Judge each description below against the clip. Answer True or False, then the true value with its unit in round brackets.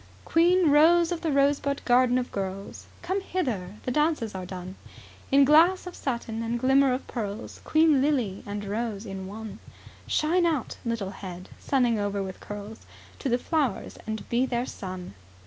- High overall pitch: True (245 Hz)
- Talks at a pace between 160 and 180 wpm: True (165 wpm)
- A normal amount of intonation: False (6.6 semitones)